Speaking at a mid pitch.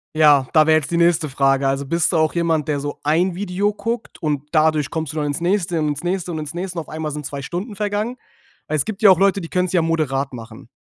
Yes: medium, 160 Hz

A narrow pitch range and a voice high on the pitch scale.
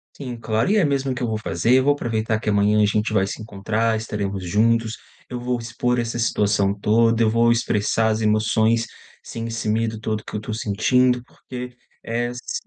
No: narrow, 2.1 semitones; low, 115 Hz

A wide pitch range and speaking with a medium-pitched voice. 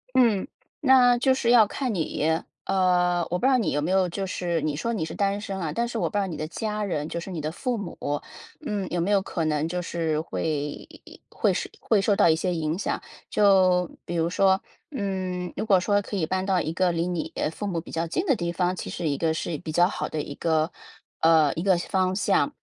No: average, 3.7 semitones; medium, 180 Hz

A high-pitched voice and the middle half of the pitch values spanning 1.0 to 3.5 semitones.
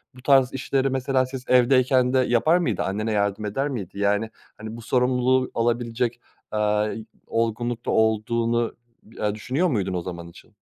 No: low, 120 Hz; average, 3.2 semitones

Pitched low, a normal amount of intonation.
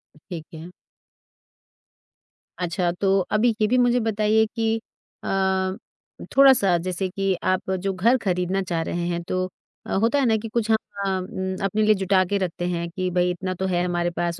No: high, 190 Hz; average, 3.2 semitones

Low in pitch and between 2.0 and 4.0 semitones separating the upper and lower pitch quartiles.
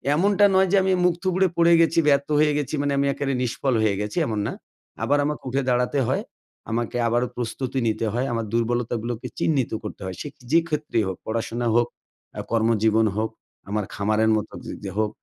No: low, 120 Hz; average, 4.7 semitones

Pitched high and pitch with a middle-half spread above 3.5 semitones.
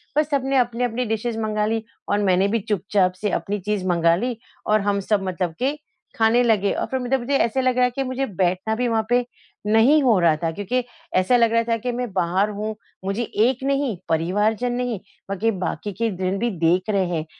Yes: high, 220 Hz; average, 4.1 semitones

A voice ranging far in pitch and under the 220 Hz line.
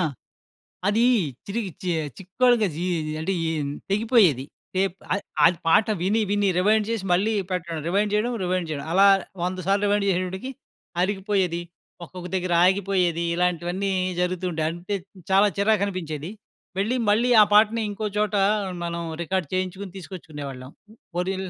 No: average, 2.7 semitones; high, 190 Hz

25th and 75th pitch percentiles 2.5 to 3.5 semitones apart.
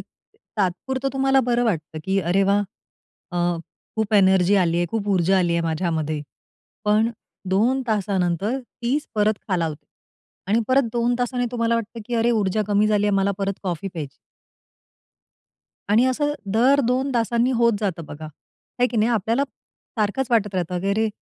No: average, 4.3 semitones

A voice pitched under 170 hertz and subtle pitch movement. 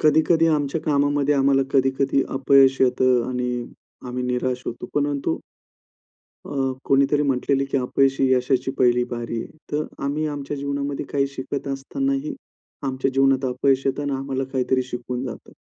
Yes: low, 135 Hz; narrow, 1.8 semitones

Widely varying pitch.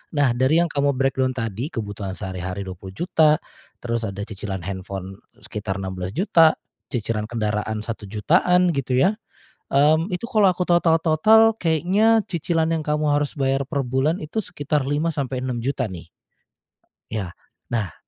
Yes: wide, 7.5 semitones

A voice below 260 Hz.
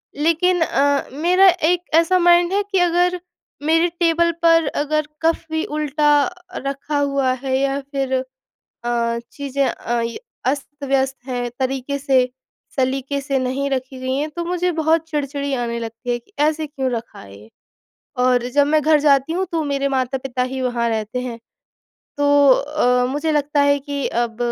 No: very high, 280 Hz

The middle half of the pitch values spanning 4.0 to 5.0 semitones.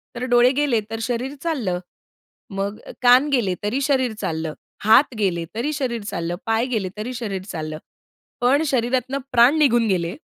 Yes: average, 4.7 semitones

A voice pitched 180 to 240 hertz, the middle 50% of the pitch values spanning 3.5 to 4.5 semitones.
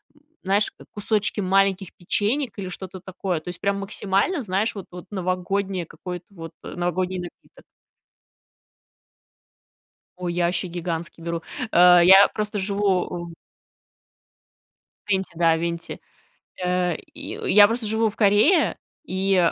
No: high, 190 Hz; narrow, 2.5 semitones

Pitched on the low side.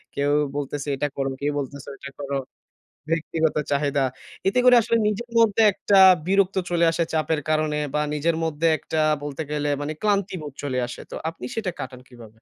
No: medium, 150 Hz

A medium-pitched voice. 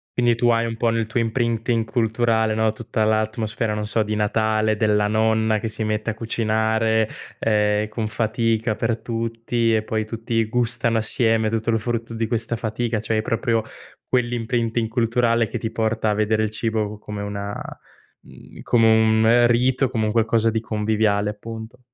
No: low, 110 Hz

